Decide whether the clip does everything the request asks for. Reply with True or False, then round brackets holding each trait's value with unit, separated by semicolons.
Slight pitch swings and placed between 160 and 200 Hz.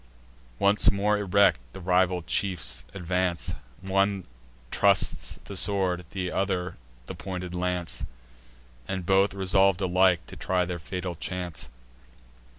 False (1.5 semitones; 90 Hz)